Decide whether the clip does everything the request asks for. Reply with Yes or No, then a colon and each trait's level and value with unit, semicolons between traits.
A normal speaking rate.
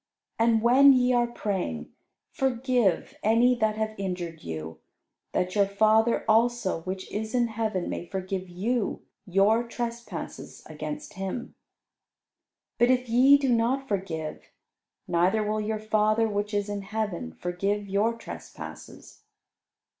No: slow, 130 wpm